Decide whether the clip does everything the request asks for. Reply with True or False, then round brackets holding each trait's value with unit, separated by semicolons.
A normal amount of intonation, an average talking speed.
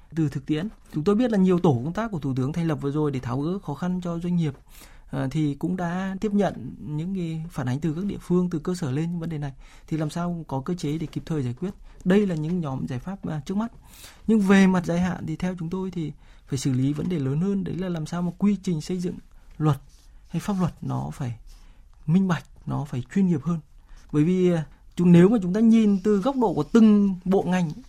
False (3.8 semitones; 255 wpm)